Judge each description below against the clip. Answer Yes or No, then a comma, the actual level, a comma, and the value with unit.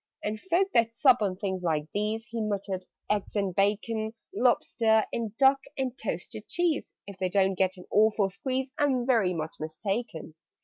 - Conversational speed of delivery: Yes, average, 175 wpm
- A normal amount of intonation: Yes, average, 4.0 semitones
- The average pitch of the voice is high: Yes, high, 215 Hz